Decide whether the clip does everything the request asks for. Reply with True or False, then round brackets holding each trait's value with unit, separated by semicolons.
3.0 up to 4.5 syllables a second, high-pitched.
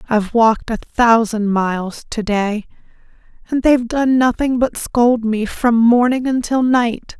True (4.3 syllables/s; 235 Hz)